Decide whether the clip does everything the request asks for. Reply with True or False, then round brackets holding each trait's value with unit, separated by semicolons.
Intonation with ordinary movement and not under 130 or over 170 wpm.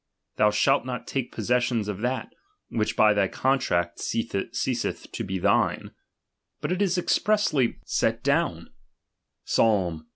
True (4.2 semitones; 140 wpm)